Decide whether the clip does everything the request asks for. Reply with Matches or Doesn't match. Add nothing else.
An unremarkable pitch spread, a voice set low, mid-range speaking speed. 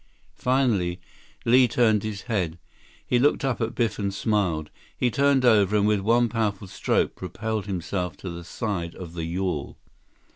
Matches